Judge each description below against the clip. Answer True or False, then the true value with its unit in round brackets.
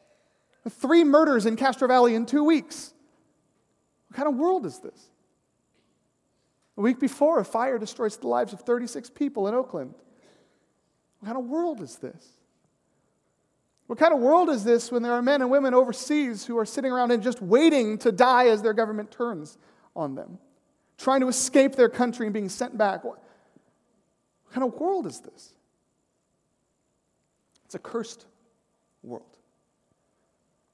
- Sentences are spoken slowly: False (155 wpm)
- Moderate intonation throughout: True (3.7 semitones)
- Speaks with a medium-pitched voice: False (250 Hz)